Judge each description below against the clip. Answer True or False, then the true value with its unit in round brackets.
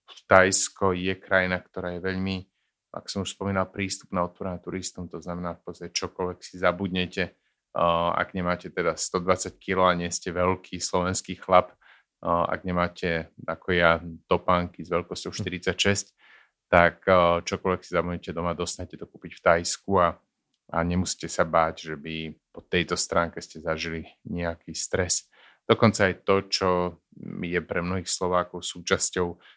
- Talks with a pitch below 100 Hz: True (90 Hz)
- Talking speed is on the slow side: False (150 wpm)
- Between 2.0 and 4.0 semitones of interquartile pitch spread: False (1.5 semitones)